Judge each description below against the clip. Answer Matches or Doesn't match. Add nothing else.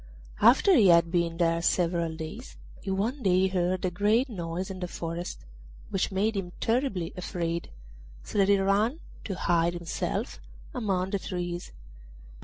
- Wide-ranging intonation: Doesn't match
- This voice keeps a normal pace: Matches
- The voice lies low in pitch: Doesn't match